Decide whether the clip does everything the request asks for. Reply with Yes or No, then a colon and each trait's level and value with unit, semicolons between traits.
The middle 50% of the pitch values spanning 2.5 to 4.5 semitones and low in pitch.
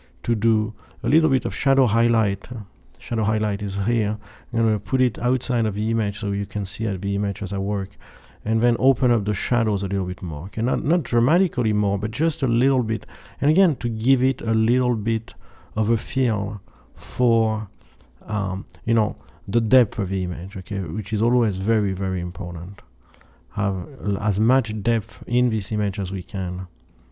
Yes: average, 3.3 semitones; low, 110 Hz